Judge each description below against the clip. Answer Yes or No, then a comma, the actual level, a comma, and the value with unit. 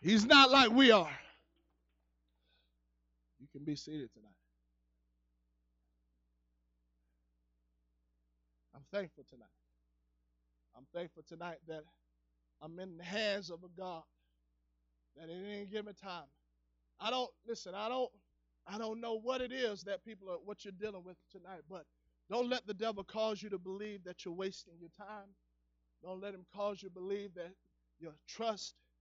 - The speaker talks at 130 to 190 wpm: Yes, average, 150 wpm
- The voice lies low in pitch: No, medium, 160 Hz